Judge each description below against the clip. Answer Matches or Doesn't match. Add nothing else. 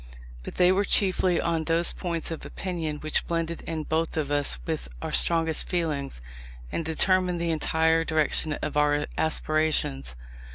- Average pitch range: Doesn't match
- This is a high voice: Doesn't match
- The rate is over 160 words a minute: Doesn't match